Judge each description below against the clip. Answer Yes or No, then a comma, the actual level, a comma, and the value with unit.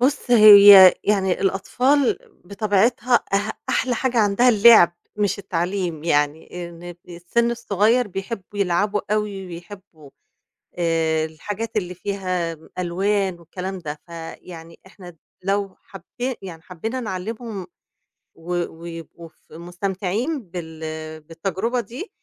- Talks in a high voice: Yes, high, 195 Hz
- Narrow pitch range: No, average, 3.7 semitones